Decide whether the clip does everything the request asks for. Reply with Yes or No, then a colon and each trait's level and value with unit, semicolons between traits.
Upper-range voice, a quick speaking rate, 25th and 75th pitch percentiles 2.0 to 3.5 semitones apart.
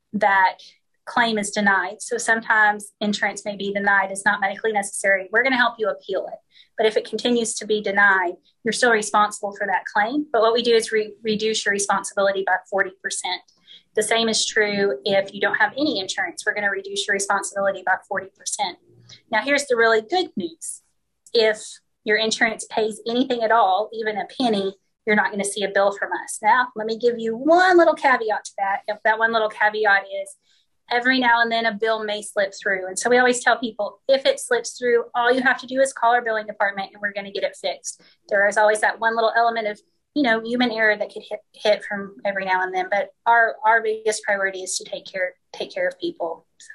Yes: high, 215 Hz; fast, 225 wpm; average, 2.8 semitones